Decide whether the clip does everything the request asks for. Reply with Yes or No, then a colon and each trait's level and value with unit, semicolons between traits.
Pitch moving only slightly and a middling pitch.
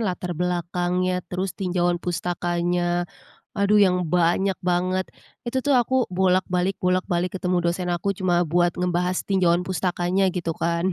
Yes: narrow, 1.2 semitones; medium, 180 Hz